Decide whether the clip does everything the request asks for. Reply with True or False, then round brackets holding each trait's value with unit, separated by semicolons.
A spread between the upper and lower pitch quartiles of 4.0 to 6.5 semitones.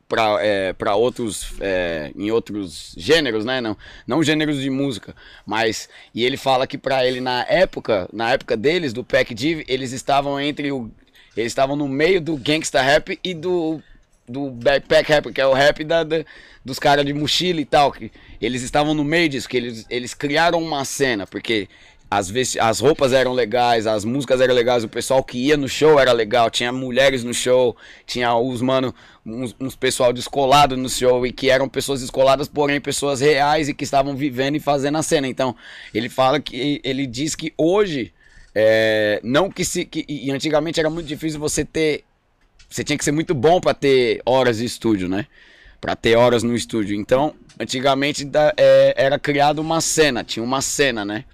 False (3.6 semitones)